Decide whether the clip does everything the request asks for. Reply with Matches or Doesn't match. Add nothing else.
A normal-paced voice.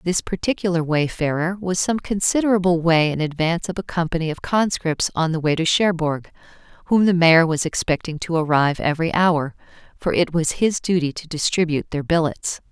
Matches